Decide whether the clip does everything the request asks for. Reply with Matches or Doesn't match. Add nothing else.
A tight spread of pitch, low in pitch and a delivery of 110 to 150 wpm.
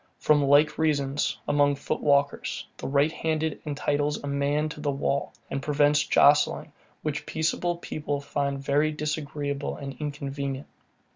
Doesn't match